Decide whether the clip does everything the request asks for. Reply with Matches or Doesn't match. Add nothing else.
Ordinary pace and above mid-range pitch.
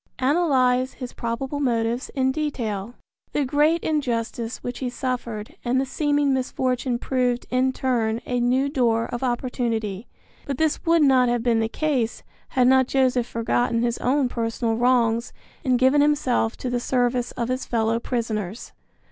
Matches